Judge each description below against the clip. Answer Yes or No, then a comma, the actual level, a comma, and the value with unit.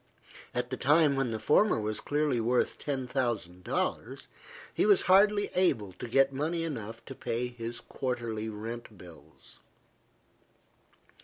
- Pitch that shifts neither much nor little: Yes, average, 4.6 semitones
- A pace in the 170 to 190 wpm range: No, average, 140 wpm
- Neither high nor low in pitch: No, low, 125 Hz